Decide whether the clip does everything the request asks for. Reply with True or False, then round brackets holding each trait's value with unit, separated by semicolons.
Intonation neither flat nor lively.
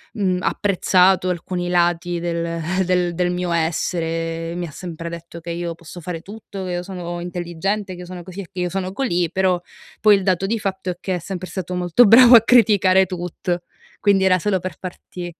False (1.8 semitones)